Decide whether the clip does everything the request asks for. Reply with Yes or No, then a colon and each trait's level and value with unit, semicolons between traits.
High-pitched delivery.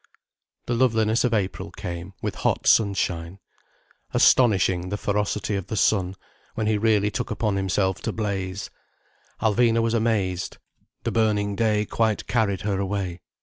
No: low, 105 Hz